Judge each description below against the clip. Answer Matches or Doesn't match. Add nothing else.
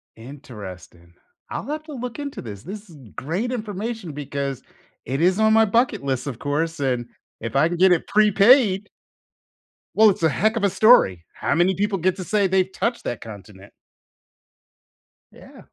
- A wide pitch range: Matches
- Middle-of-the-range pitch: Matches